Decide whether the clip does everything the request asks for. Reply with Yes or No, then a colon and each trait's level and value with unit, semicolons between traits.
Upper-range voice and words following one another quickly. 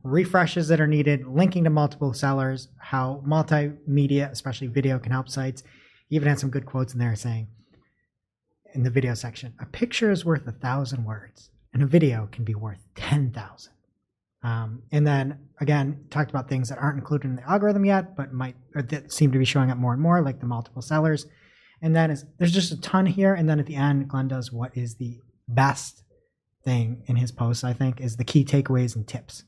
No: low, 135 Hz; fast, 210 wpm